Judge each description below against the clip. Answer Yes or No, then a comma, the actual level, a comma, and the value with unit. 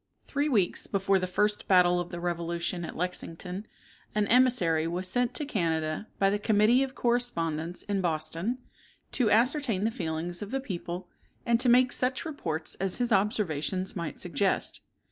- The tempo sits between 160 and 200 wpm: Yes, average, 165 wpm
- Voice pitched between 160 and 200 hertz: Yes, high, 190 Hz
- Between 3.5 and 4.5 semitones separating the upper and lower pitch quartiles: No, wide, 5.5 semitones